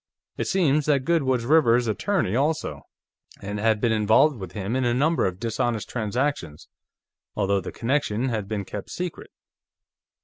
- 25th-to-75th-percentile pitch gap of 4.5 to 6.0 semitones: Yes, wide, 5.4 semitones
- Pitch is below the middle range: Yes, low, 120 Hz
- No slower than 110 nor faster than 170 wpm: Yes, average, 160 wpm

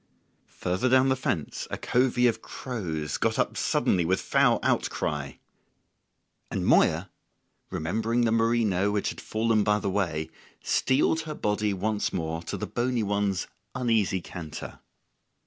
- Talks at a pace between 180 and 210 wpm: No, average, 140 wpm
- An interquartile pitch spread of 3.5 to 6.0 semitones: Yes, average, 4.7 semitones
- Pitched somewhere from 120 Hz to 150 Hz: No, low, 105 Hz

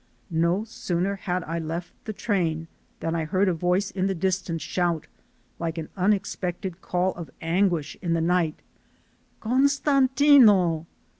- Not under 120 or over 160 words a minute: Yes, average, 140 wpm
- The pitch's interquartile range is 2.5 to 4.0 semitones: Yes, average, 3.0 semitones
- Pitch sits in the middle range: Yes, medium, 180 Hz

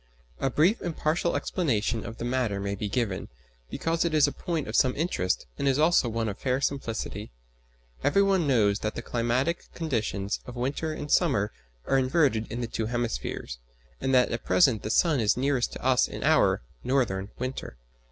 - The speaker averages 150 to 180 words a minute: No, average, 190 wpm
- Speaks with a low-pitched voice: Yes, low, 125 Hz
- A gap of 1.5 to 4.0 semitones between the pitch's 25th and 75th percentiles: No, average, 5.0 semitones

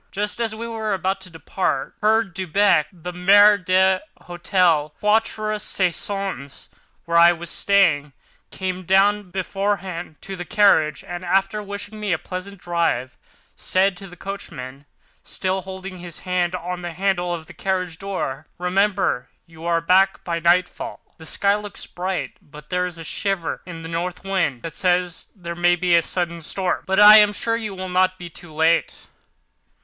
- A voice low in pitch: No, medium, 185 Hz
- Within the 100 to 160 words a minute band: No, average, 170 wpm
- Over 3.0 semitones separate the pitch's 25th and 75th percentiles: No, narrow, 2.6 semitones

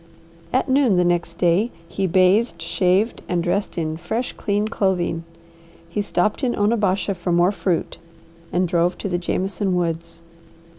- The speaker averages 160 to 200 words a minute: No, average, 150 wpm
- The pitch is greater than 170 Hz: Yes, medium, 185 Hz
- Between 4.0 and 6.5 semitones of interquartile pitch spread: No, average, 2.9 semitones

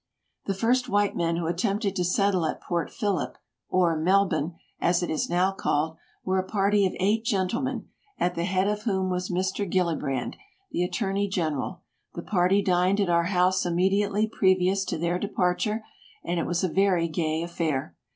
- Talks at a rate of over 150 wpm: Yes, average, 180 wpm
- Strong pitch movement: No, narrow, 2.5 semitones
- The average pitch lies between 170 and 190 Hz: Yes, medium, 185 Hz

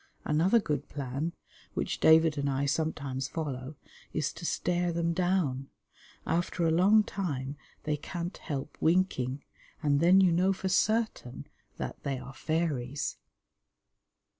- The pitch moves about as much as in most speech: Yes, average, 4.0 semitones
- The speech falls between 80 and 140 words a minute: Yes, slow, 135 wpm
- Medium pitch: Yes, medium, 160 Hz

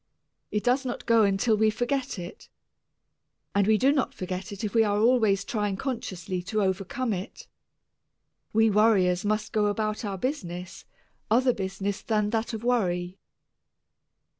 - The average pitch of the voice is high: Yes, high, 210 Hz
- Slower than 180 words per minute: Yes, average, 150 wpm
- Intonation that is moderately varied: Yes, average, 3.0 semitones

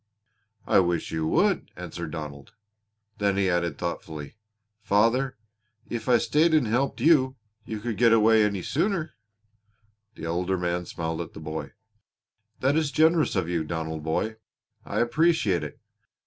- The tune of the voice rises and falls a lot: Yes, wide, 7.4 semitones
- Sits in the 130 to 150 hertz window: No, low, 100 Hz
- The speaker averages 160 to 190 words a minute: No, average, 150 wpm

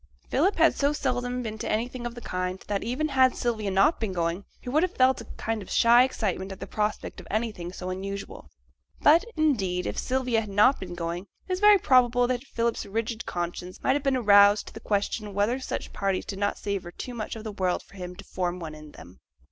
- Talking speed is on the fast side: Yes, fast, 230 wpm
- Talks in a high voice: Yes, high, 215 Hz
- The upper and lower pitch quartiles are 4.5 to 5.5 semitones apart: Yes, average, 4.8 semitones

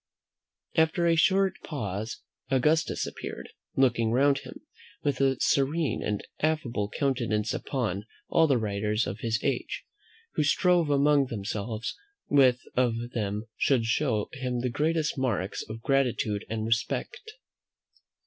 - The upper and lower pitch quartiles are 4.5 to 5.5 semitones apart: Yes, average, 4.8 semitones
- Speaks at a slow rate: Yes, slow, 130 wpm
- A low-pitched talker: Yes, low, 125 Hz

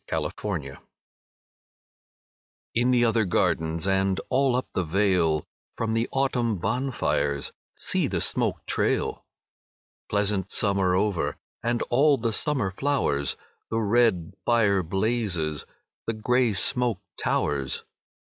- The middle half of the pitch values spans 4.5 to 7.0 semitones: Yes, average, 5.0 semitones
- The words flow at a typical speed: No, slow, 120 wpm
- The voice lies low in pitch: Yes, low, 105 Hz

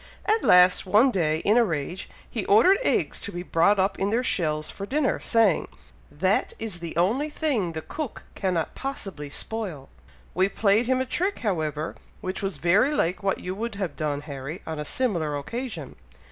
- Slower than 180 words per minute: No, average, 185 wpm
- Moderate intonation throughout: No, wide, 6.0 semitones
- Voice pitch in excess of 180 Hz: Yes, high, 190 Hz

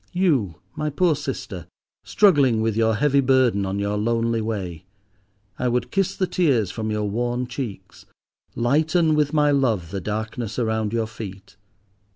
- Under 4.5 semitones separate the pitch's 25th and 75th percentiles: No, average, 5.1 semitones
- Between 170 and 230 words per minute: No, average, 155 wpm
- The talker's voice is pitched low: Yes, low, 115 Hz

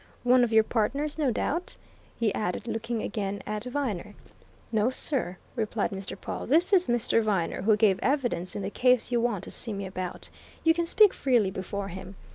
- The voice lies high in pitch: Yes, high, 225 Hz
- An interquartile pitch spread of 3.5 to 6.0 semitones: Yes, average, 4.2 semitones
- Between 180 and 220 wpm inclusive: Yes, average, 190 wpm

